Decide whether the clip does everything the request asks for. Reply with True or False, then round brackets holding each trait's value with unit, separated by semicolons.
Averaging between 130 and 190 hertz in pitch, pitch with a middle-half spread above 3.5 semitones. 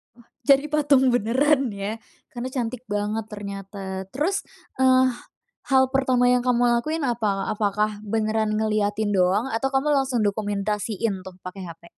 False (220 Hz; 4.1 semitones)